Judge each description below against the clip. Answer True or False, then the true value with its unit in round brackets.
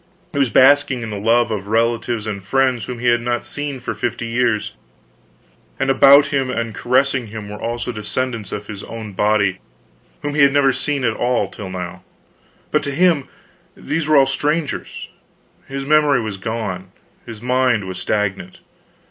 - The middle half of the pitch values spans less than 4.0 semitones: False (4.3 semitones)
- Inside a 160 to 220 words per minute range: True (175 wpm)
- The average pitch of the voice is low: True (120 Hz)